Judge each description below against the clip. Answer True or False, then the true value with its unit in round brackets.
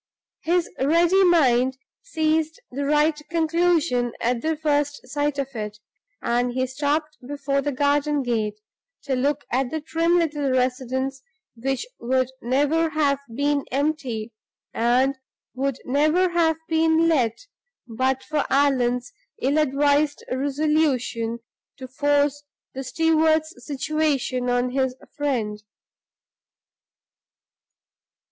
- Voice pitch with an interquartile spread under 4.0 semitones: True (3.4 semitones)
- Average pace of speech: False (110 wpm)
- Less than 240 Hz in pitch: False (285 Hz)